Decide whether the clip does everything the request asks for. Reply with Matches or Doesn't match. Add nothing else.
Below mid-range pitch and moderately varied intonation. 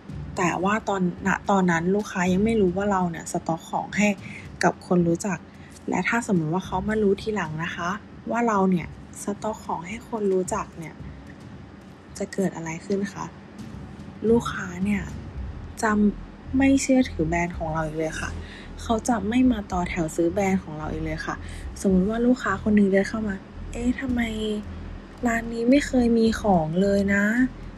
Doesn't match